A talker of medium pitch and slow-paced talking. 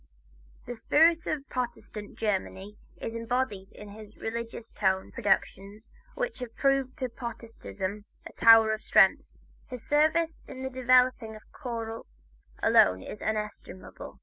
No: high, 230 Hz; slow, 125 wpm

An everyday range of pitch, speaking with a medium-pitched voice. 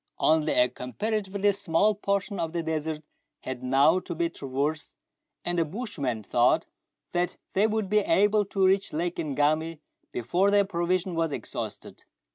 Yes: average, 4.6 semitones; medium, 170 Hz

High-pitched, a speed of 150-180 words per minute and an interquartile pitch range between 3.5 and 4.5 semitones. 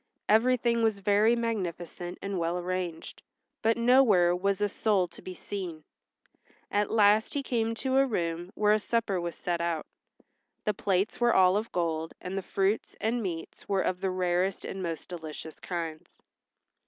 Yes: high, 195 Hz; average, 165 wpm; average, 3.9 semitones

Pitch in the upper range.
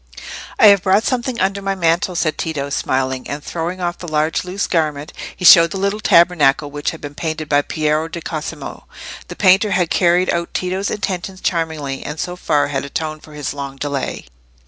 No: medium, 165 Hz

